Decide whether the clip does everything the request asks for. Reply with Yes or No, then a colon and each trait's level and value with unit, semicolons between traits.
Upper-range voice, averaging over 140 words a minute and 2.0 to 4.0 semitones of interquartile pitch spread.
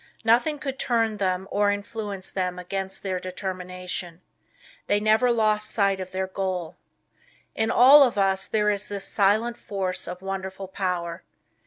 Yes: high, 195 Hz; average, 150 wpm; narrow, 2.5 semitones